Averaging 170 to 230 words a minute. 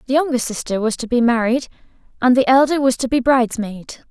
Yes: fast, 205 wpm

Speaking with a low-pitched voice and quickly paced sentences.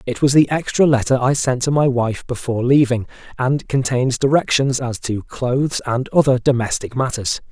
No: low, 130 Hz; average, 175 wpm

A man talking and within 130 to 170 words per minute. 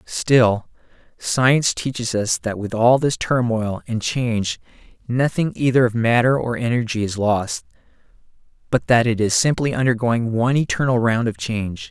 Yes: male; average, 150 wpm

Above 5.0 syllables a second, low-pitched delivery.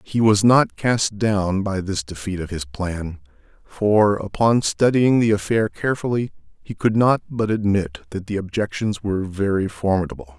No: 4.6 syllables/s; low, 100 Hz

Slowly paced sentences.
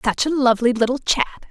No: average, 200 wpm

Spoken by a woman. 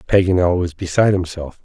No: male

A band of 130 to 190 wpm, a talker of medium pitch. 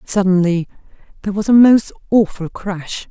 No: slow, 135 wpm; high, 195 Hz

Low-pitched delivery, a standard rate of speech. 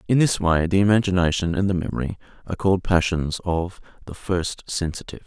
Yes: very low, 90 Hz; average, 170 wpm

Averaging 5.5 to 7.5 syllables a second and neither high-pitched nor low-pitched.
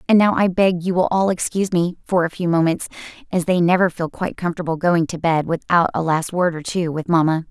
Yes: 5.9 syllables/s; medium, 175 Hz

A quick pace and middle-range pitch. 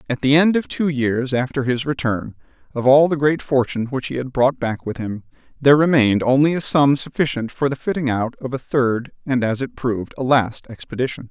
No: fast, 220 wpm; low, 130 Hz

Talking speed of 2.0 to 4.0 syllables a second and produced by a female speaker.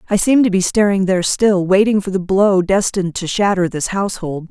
No: 5.6 syllables/s; female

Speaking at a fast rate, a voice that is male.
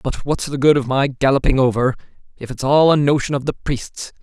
Yes: fast, 225 wpm; male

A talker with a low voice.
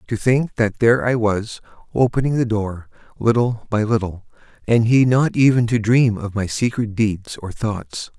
Yes: low, 110 Hz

